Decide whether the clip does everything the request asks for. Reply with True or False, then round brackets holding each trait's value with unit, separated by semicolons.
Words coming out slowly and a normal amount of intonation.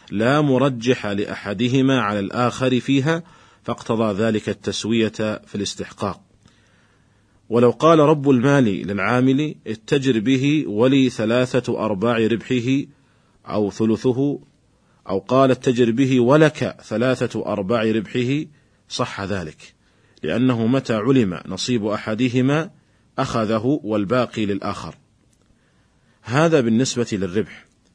False (95 wpm; 3.5 semitones)